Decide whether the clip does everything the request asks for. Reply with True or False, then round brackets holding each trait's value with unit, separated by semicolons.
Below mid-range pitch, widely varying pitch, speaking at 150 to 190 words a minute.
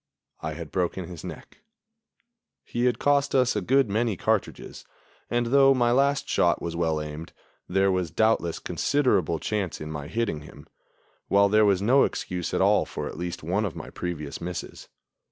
True (95 Hz; 6.1 semitones; 175 wpm)